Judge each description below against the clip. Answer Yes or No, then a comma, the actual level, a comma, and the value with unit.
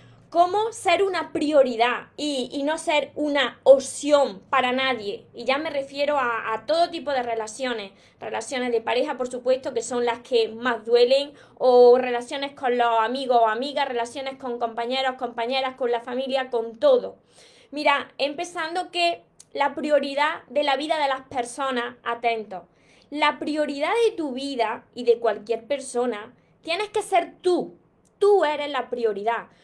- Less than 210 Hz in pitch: No, very high, 265 Hz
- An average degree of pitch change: Yes, average, 3.8 semitones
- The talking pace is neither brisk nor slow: Yes, average, 160 wpm